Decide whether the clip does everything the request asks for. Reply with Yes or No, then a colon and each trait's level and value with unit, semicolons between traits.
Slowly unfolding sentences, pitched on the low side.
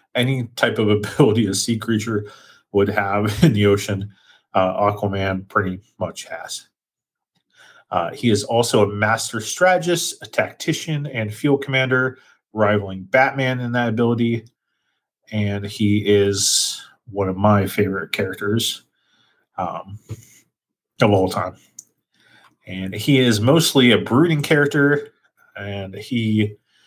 Yes: slow, 125 wpm; low, 110 Hz